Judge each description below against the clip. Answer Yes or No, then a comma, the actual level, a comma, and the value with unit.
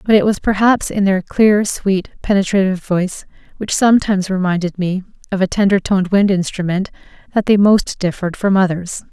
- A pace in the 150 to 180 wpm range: Yes, average, 170 wpm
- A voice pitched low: No, high, 195 Hz